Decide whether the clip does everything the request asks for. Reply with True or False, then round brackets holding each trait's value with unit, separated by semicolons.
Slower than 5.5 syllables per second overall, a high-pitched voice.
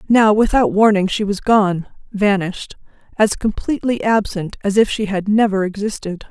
True (5.0 syllables/s; 205 Hz)